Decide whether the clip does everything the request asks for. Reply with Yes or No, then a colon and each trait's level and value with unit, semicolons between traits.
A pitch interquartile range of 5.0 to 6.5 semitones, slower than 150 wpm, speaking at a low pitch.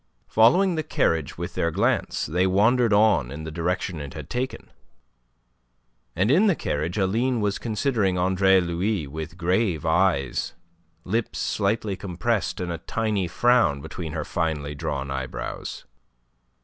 Yes: wide, 5.6 semitones; average, 140 wpm; very low, 95 Hz